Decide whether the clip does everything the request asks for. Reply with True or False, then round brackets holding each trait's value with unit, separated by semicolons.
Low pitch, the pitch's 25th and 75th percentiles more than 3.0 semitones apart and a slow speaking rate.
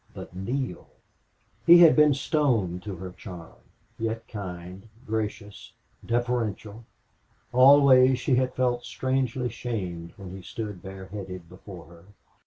True (110 Hz; 5.4 semitones; 120 wpm)